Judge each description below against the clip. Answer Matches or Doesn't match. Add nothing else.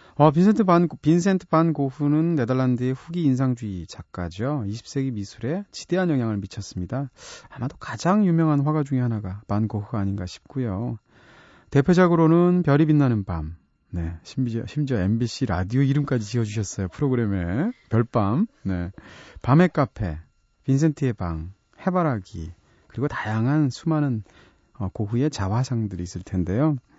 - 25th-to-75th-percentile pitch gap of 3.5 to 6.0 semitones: Doesn't match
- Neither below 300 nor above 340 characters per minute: Matches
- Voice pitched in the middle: Doesn't match